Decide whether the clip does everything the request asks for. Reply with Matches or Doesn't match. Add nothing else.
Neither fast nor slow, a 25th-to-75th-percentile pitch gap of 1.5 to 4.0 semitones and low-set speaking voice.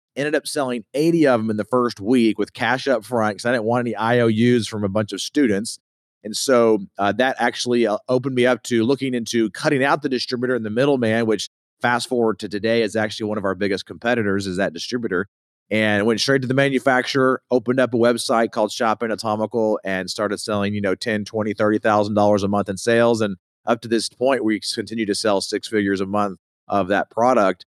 Doesn't match